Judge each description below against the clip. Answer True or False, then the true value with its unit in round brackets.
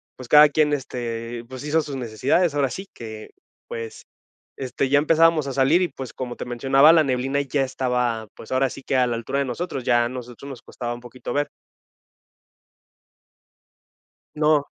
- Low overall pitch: True (130 Hz)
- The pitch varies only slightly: False (3.2 semitones)